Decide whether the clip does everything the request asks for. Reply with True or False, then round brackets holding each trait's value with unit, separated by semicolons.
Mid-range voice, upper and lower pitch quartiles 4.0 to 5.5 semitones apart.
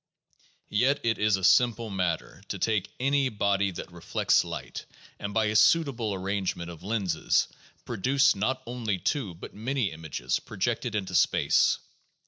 False (105 Hz; 4.3 semitones)